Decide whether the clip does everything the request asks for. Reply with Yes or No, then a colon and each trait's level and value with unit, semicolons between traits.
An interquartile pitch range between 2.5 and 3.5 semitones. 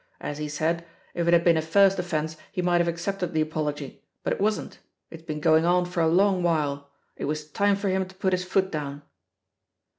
Yes: average, 3.1 semitones